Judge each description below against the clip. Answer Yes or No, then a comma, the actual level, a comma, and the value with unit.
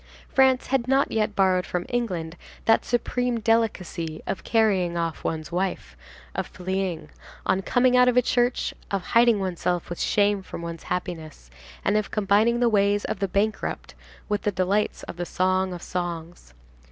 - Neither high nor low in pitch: No, high, 195 Hz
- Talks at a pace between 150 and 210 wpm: Yes, average, 165 wpm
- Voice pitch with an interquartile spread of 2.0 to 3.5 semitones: No, average, 4.3 semitones